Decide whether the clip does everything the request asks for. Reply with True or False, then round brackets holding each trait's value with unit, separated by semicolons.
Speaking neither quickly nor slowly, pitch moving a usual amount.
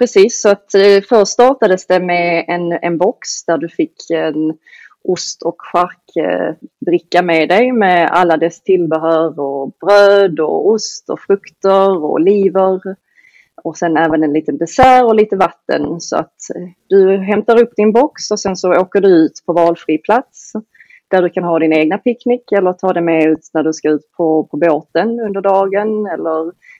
True (170 wpm; 4.1 semitones)